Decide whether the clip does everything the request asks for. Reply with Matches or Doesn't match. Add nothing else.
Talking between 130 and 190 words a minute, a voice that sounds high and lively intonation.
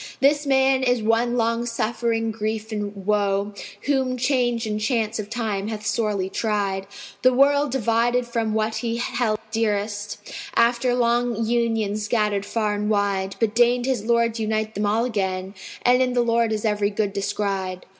Doesn't match